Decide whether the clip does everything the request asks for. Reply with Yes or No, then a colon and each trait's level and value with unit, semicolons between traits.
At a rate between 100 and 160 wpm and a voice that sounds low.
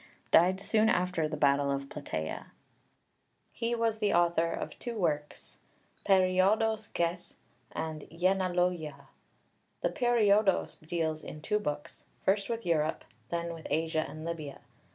No: slow, 135 wpm; medium, 170 Hz